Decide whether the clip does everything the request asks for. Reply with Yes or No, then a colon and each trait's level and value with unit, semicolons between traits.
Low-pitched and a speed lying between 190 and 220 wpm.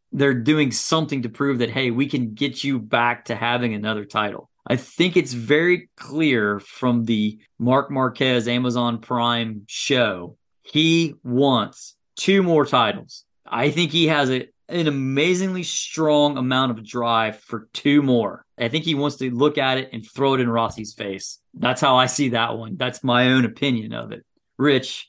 No: low, 130 Hz; average, 175 wpm